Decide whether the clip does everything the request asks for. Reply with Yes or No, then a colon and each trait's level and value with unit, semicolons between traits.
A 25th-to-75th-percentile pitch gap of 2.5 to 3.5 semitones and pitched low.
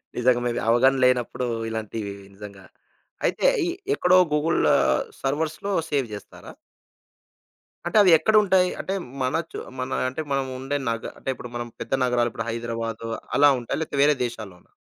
No: average, 4.6 semitones; low, 125 Hz